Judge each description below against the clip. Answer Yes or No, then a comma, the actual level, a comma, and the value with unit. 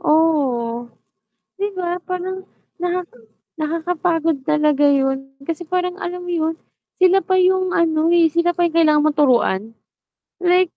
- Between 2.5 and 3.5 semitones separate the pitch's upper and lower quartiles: Yes, average, 3.2 semitones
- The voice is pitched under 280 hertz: No, very high, 330 Hz